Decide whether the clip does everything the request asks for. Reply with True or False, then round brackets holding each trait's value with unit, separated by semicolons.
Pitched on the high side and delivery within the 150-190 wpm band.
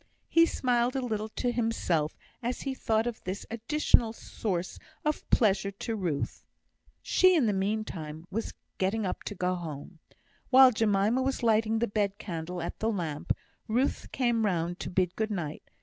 True (215 Hz; 165 wpm)